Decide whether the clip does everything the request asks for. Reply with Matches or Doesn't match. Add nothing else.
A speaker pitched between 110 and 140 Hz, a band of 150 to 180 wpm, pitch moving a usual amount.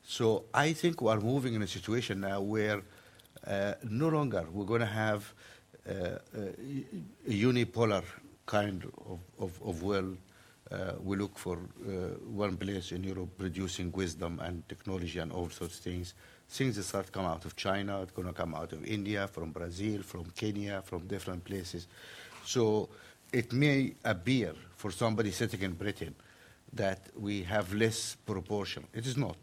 Doesn't match